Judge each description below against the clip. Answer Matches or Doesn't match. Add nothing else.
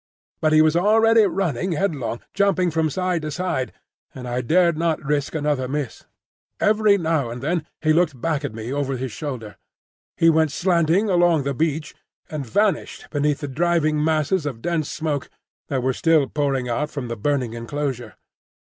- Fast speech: Doesn't match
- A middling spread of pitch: Matches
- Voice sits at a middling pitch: Matches